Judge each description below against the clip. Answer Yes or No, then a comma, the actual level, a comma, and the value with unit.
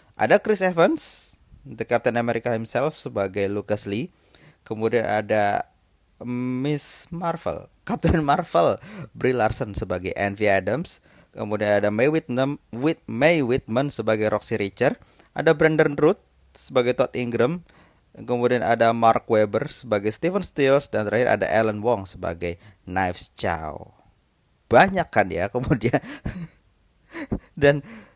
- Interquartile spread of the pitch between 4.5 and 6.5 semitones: Yes, average, 5.1 semitones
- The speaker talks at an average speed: Yes, average, 120 wpm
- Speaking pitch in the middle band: No, low, 115 Hz